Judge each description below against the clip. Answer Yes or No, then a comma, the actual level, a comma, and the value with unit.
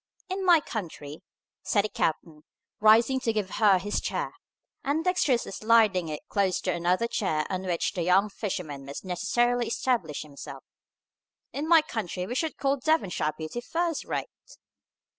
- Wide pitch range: Yes, wide, 6.2 semitones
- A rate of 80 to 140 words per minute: No, average, 155 wpm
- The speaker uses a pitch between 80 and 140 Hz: No, high, 210 Hz